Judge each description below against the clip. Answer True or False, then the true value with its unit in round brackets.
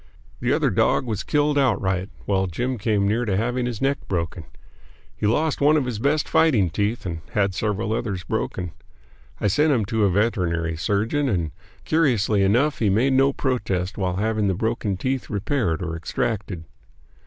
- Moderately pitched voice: False (105 Hz)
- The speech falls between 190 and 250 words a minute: False (175 wpm)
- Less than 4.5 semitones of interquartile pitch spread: False (5.1 semitones)